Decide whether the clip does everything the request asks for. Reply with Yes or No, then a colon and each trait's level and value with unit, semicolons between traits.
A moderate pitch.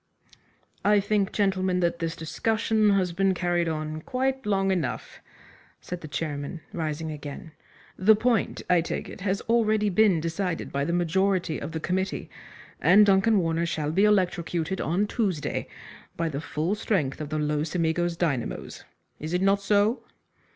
Yes: medium, 180 Hz